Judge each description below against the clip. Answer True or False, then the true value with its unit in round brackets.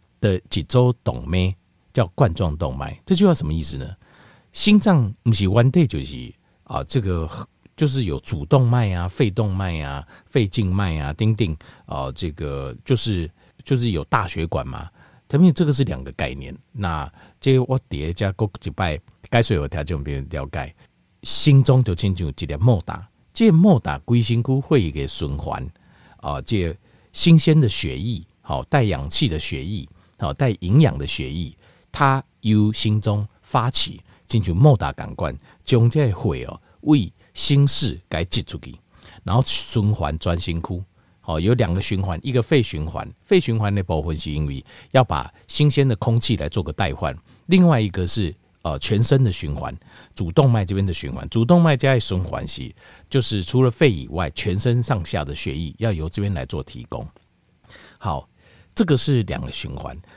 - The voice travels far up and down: True (6.9 semitones)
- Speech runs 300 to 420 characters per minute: False (250 characters per minute)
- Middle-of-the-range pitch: False (105 Hz)